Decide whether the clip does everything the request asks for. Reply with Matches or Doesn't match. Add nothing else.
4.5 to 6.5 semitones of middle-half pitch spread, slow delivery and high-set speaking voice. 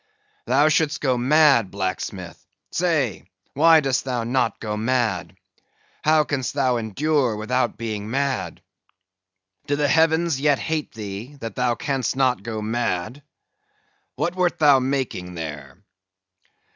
Doesn't match